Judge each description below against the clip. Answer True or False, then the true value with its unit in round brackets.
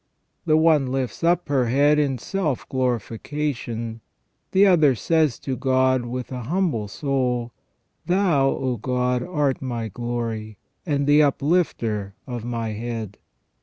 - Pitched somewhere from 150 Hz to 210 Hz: False (130 Hz)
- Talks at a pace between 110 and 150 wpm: True (135 wpm)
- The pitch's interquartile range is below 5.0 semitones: True (4.0 semitones)